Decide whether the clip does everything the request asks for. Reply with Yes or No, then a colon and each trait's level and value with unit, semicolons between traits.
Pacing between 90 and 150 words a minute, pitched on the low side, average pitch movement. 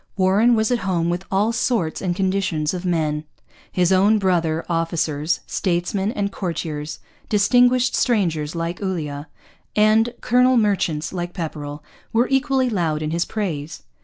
No: average, 140 wpm; medium, 185 Hz; average, 4.8 semitones